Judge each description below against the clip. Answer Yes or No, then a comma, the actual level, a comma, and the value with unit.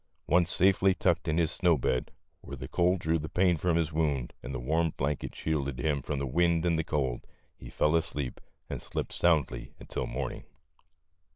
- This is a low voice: Yes, very low, 80 Hz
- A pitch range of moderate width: Yes, average, 3.6 semitones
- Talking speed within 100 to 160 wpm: No, average, 185 wpm